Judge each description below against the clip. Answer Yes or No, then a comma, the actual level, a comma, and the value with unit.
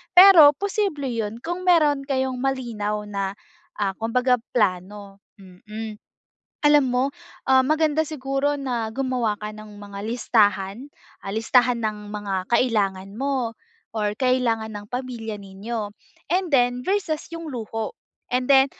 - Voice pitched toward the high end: Yes, high, 240 Hz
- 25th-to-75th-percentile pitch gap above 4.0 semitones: Yes, average, 4.6 semitones